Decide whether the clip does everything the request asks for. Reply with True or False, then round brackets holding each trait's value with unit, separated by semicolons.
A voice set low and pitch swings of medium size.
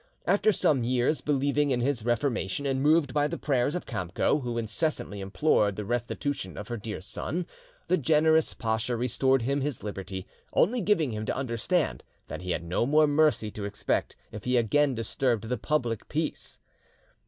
True (125 Hz; 5.0 semitones)